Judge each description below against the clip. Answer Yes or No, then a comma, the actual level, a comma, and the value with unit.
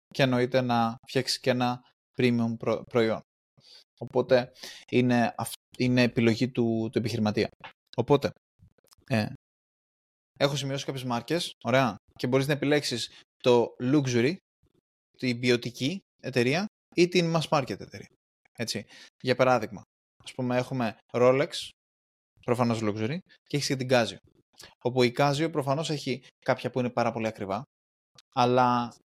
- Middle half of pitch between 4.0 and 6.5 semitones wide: No, narrow, 2.6 semitones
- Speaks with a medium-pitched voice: No, low, 125 Hz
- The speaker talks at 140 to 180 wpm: No, average, 130 wpm